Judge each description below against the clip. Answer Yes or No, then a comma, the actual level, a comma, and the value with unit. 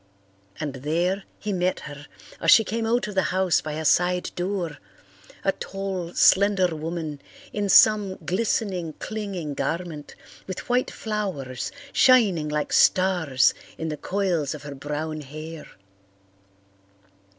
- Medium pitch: Yes, medium, 175 Hz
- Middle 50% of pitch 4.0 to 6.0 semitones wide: Yes, average, 4.5 semitones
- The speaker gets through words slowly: Yes, slow, 130 wpm